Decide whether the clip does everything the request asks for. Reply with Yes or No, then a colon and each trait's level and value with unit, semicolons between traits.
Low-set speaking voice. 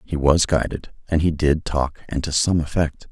Yes: very low, 75 Hz